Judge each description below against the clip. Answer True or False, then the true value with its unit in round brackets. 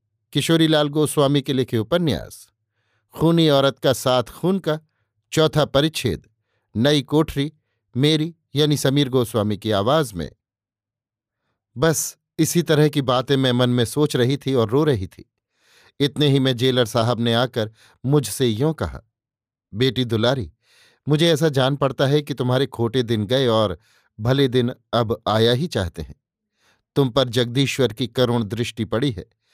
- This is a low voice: True (130 Hz)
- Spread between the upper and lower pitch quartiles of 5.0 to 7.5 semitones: False (4.1 semitones)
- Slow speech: False (150 wpm)